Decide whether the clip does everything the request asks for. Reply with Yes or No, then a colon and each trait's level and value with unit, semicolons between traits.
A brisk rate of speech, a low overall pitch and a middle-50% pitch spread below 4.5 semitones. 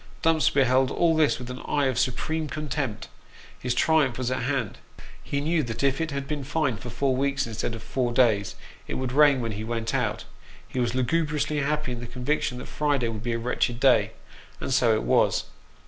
Yes: fast, 210 wpm; low, 130 Hz; average, 3.4 semitones